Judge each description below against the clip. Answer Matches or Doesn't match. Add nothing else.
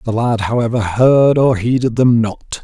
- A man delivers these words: Matches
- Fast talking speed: Doesn't match